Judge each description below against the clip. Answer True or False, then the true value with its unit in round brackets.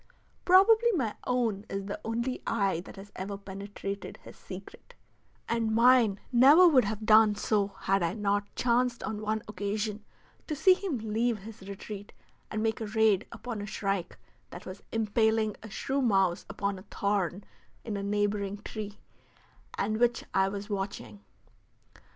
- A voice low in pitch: False (210 Hz)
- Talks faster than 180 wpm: False (155 wpm)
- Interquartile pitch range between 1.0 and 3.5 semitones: True (2.5 semitones)